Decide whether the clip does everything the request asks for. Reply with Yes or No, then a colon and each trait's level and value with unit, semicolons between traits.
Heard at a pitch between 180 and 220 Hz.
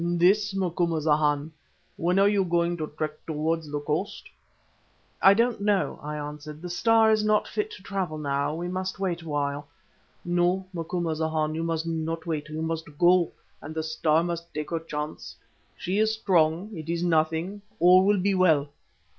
No: medium, 165 Hz